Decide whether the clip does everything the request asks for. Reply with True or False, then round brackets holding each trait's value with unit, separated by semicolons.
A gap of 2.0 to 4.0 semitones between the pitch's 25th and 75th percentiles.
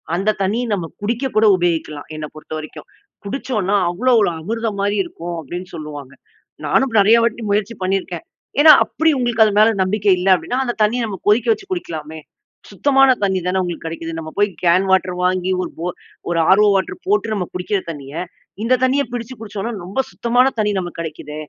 False (4.7 semitones)